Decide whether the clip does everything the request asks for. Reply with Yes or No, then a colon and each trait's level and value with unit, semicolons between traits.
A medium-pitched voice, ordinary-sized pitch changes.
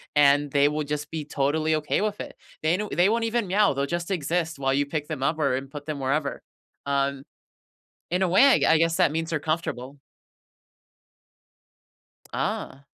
Yes: medium, 155 Hz; average, 3.2 semitones